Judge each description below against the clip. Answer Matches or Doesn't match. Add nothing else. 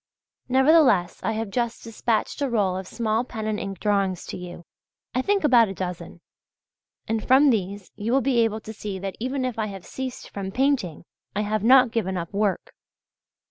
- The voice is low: Doesn't match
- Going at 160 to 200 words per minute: Matches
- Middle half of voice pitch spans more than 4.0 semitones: Matches